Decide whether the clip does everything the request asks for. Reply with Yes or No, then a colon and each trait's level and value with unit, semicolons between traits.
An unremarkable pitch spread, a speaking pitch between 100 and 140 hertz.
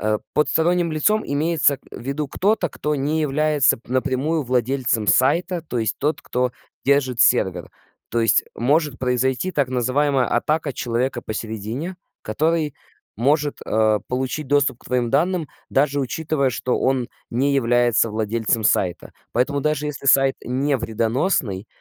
Yes: average, 3.9 semitones; low, 135 Hz